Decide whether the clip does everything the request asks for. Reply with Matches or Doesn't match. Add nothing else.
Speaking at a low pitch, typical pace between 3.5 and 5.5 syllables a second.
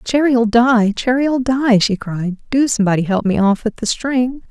Doesn't match